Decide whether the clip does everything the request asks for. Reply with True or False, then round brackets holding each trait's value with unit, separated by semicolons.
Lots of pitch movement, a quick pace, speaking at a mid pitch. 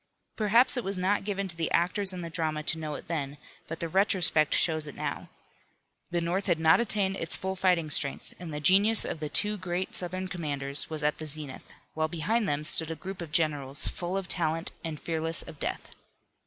False (3.5 semitones; 210 wpm; 170 Hz)